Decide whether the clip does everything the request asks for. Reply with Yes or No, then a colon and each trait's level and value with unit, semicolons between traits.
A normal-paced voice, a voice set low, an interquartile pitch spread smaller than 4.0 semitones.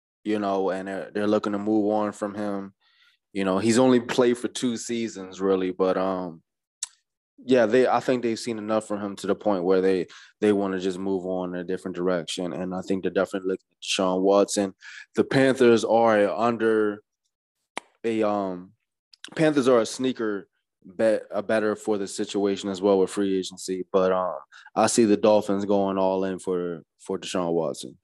Yes: average, 195 wpm; low, 100 Hz; narrow, 2.4 semitones